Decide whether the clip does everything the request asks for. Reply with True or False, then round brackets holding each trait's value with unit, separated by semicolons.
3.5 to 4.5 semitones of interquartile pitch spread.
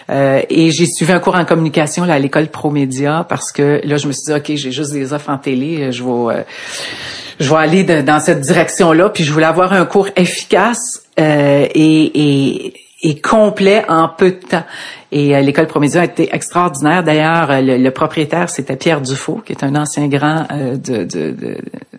False (3.0 semitones)